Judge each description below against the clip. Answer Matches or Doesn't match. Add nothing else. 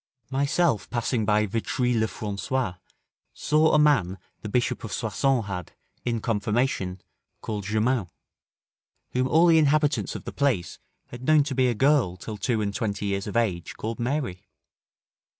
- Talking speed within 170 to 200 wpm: Doesn't match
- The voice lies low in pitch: Matches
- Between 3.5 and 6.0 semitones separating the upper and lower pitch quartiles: Matches